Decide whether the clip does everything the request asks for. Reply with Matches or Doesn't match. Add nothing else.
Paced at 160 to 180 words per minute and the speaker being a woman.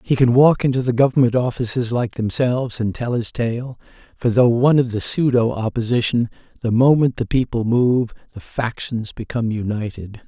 Doesn't match